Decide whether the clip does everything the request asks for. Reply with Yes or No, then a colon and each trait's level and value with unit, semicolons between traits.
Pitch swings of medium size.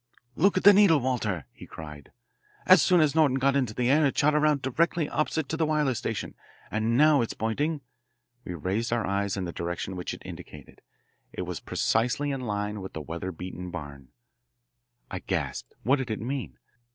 No: wide, 7.9 semitones